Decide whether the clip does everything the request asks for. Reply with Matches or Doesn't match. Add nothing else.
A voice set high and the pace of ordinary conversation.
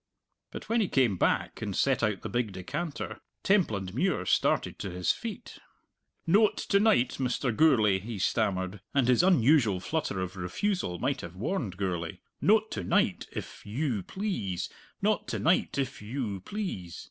Doesn't match